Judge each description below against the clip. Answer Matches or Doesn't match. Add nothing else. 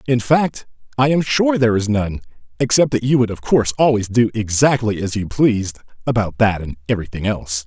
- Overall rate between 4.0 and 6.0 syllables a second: Matches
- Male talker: Matches